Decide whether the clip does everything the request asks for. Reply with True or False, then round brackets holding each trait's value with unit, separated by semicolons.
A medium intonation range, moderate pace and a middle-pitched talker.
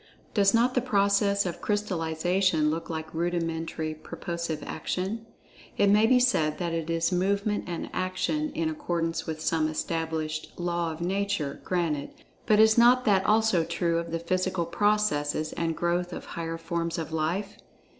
True (3.6 semitones; 155 wpm; 170 Hz)